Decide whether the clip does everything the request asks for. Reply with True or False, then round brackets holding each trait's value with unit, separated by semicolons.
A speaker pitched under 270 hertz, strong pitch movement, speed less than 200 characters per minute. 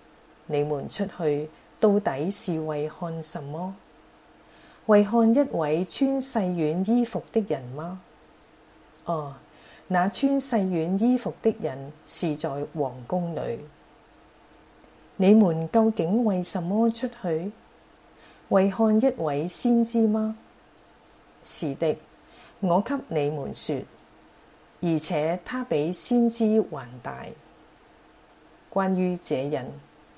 True (185 Hz; 6.0 semitones; 145 characters per minute)